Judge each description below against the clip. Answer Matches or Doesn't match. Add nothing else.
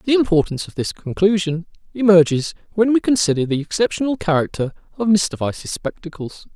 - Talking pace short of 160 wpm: Matches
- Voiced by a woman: Doesn't match